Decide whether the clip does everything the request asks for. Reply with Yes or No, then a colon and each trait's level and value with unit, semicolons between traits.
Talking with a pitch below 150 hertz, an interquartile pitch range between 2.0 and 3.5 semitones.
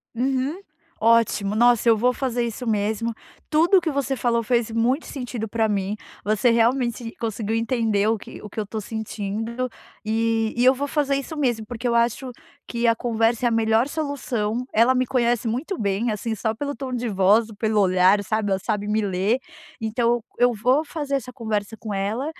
No: high, 230 Hz; narrow, 2.6 semitones